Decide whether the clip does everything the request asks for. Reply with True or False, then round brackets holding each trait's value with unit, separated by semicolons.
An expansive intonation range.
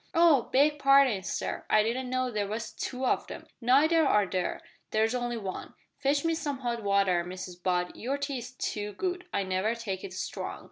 True (5.7 semitones)